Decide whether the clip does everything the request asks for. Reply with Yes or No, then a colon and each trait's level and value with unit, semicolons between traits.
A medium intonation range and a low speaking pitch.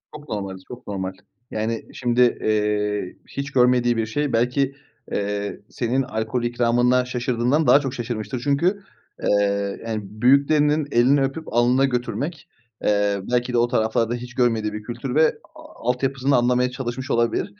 Yes: average, 3.3 semitones; low, 120 Hz